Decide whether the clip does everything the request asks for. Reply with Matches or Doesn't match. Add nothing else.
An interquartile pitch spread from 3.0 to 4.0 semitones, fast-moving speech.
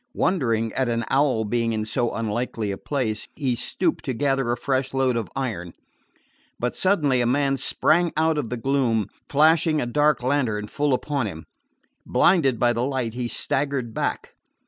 Doesn't match